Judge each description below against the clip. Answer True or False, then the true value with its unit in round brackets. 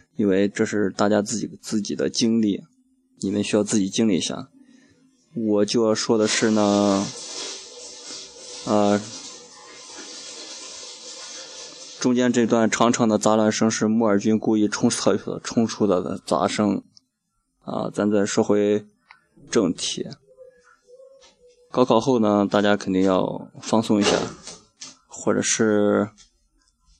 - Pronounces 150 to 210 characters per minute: True (175 characters per minute)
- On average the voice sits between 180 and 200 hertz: False (110 Hz)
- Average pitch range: False (7.1 semitones)